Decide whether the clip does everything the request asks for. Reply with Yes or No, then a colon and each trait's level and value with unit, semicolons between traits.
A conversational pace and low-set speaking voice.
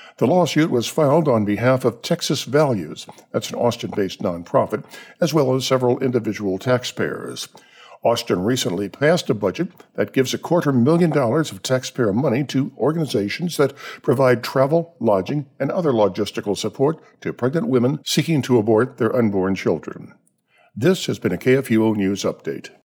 Yes: average, 155 wpm; low, 130 Hz